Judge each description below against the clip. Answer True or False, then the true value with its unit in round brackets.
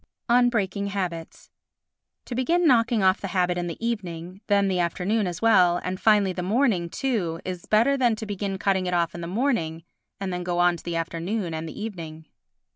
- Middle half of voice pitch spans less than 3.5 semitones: False (4.1 semitones)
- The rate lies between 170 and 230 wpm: True (200 wpm)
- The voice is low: False (185 Hz)